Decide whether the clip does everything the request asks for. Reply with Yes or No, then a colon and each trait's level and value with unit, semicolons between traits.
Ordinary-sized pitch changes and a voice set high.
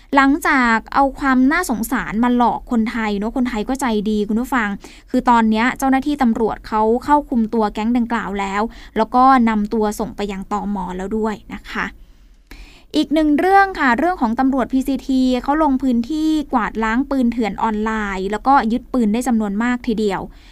Yes: average, 3.4 semitones; high, 235 Hz